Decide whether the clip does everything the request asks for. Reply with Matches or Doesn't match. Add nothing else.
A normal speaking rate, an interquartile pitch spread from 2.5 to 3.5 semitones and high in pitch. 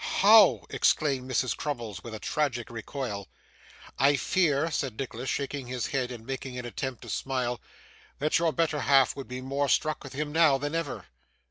Doesn't match